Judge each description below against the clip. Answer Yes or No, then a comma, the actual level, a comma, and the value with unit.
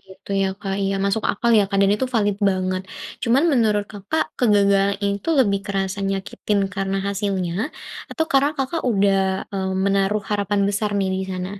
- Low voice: No, high, 200 Hz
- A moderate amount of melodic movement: No, narrow, 1.4 semitones